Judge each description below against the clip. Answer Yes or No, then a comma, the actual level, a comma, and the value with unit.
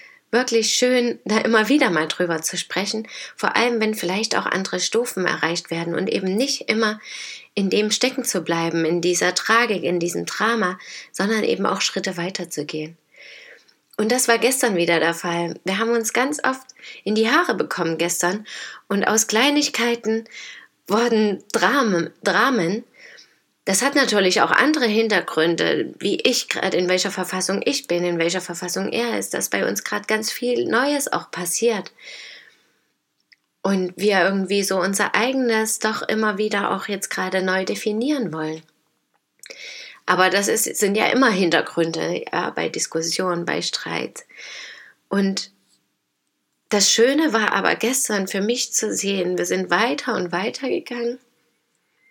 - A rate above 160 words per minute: No, average, 150 wpm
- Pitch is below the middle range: No, high, 205 Hz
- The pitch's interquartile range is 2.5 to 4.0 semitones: No, average, 4.7 semitones